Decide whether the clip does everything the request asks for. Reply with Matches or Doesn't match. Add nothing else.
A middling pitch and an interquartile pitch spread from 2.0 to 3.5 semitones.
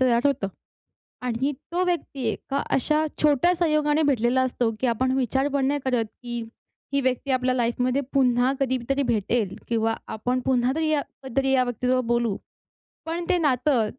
Doesn't match